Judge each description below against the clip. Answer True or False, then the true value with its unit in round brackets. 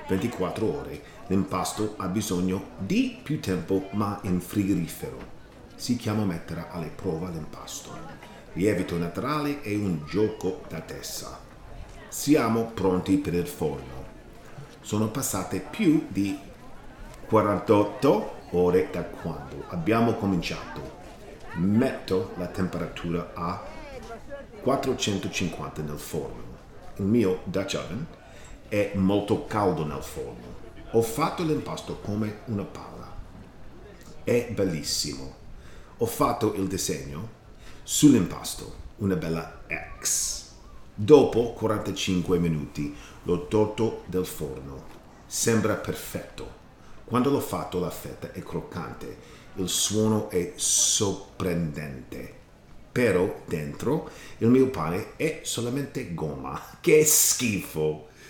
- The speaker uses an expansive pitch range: False (4.3 semitones)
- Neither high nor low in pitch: False (100 Hz)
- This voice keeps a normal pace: False (105 wpm)